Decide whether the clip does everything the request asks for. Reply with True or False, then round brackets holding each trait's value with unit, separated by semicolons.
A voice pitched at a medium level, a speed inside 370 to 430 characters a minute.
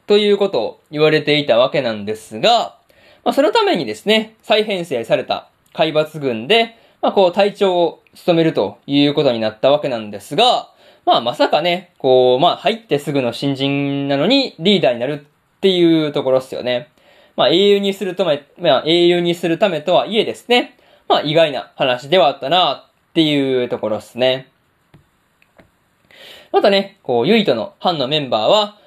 False (165 Hz; 335 characters per minute)